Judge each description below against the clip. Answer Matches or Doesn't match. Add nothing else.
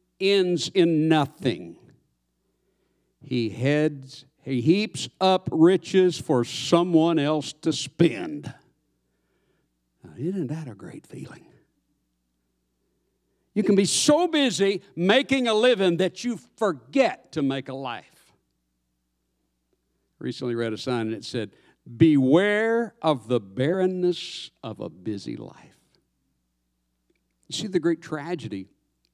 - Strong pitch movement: Matches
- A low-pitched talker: Doesn't match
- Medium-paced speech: Doesn't match